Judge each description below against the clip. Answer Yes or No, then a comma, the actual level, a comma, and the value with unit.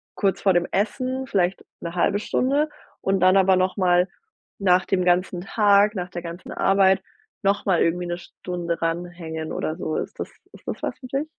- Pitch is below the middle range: No, medium, 185 Hz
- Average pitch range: No, narrow, 2.3 semitones